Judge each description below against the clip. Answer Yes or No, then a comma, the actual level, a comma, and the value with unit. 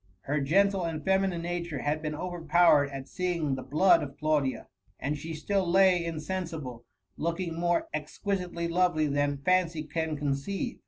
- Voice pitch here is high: No, medium, 165 Hz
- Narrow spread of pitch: No, average, 3.4 semitones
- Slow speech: No, average, 150 wpm